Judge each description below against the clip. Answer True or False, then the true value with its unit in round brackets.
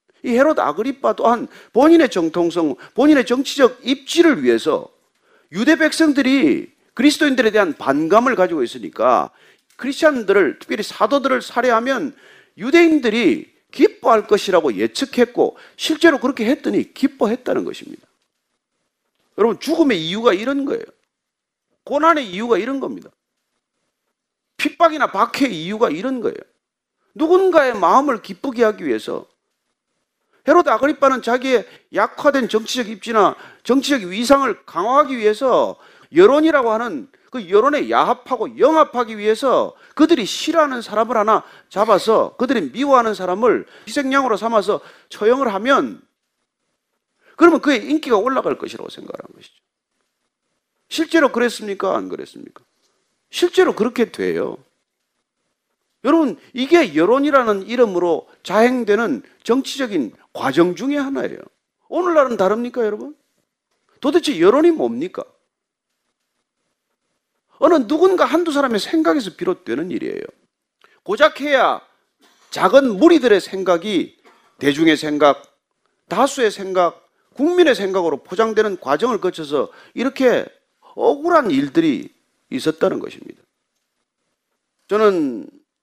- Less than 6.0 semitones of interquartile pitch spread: True (5.6 semitones)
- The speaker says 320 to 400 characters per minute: False (300 characters per minute)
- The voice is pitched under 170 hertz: False (270 Hz)